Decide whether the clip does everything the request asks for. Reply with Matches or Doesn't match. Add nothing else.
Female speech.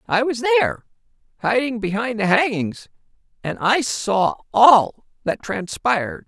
Doesn't match